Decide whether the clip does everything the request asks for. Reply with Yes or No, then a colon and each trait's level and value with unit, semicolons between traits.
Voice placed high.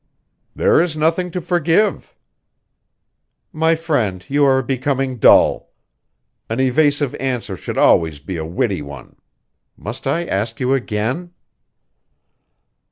No: low, 135 Hz